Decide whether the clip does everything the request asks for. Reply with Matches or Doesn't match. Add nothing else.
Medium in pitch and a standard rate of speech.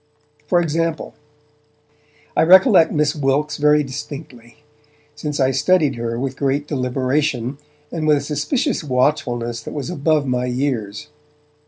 Doesn't match